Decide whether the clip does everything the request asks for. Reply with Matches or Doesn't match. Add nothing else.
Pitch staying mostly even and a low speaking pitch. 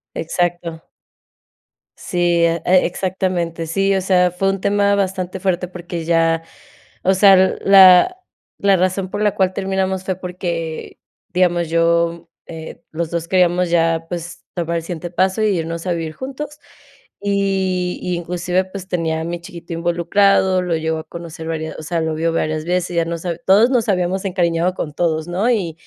Doesn't match